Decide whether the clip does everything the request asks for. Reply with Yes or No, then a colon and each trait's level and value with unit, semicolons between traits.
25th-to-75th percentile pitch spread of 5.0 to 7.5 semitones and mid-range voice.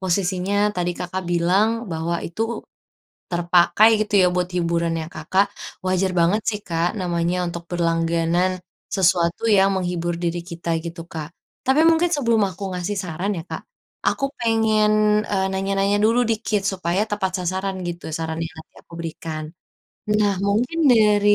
No: average, 3.3 semitones; medium, 180 Hz